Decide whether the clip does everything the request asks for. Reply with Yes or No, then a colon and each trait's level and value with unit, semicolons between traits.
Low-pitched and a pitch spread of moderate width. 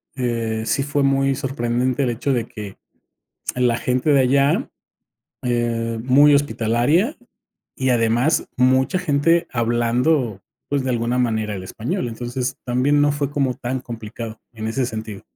Yes: low, 125 Hz; average, 3.0 semitones